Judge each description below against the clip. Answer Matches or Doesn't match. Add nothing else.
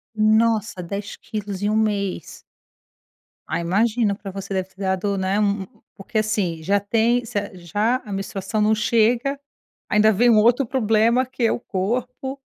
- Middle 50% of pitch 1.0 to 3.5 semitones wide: Matches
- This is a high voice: Matches